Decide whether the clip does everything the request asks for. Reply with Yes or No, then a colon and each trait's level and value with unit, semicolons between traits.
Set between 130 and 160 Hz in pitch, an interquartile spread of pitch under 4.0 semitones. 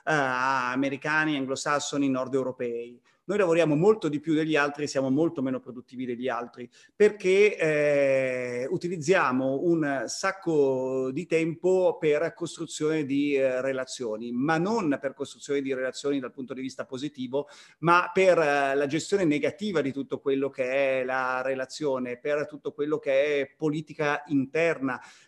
Yes: medium, 140 Hz; average, 3.2 semitones